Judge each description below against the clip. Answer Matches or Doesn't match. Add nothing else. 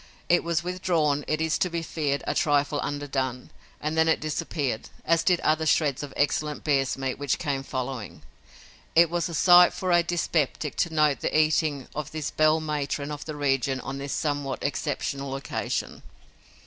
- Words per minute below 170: Doesn't match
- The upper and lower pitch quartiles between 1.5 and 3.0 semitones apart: Matches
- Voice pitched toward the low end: Doesn't match